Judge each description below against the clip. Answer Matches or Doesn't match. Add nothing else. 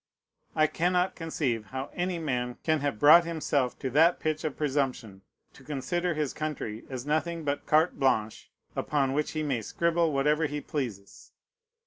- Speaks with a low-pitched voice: Doesn't match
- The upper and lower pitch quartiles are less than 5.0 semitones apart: Matches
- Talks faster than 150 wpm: Matches